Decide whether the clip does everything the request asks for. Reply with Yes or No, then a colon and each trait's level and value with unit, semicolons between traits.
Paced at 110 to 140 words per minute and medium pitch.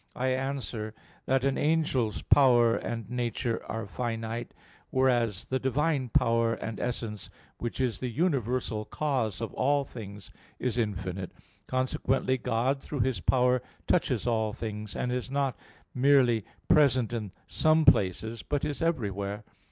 No: slow, 135 wpm; low, 120 Hz